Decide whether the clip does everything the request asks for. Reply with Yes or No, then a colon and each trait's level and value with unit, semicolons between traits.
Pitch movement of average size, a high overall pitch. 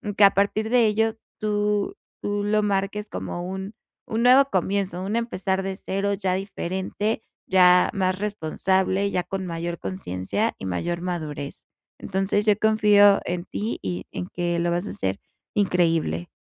Yes: average, 3.1 semitones; high, 195 Hz